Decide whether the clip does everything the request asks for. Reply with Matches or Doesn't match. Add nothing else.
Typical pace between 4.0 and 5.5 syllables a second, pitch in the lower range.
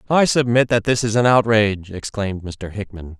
Matches